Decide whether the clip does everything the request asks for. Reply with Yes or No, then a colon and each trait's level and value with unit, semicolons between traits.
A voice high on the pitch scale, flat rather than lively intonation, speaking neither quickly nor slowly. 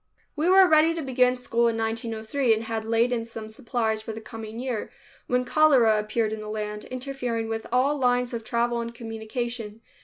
Yes: high, 235 Hz; narrow, 2.2 semitones; average, 190 wpm